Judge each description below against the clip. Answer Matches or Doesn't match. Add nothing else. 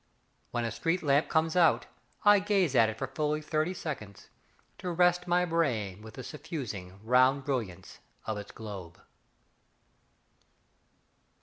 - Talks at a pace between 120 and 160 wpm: Matches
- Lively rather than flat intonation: Matches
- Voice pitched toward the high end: Doesn't match